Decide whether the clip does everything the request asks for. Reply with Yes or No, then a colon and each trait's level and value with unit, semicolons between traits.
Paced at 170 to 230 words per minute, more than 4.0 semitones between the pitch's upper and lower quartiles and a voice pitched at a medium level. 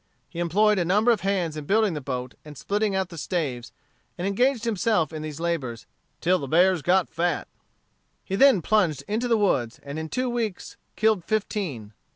Yes: average, 190 wpm; wide, 5.4 semitones; medium, 180 Hz